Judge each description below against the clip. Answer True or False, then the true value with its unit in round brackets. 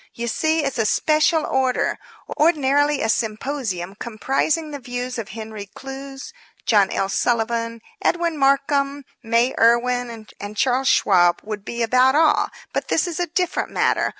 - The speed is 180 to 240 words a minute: False (150 wpm)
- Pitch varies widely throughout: False (4.2 semitones)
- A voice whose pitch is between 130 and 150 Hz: False (250 Hz)